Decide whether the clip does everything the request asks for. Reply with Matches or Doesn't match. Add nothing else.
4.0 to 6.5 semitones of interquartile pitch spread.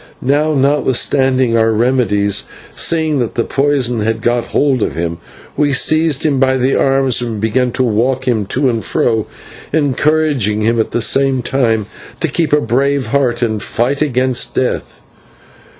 Doesn't match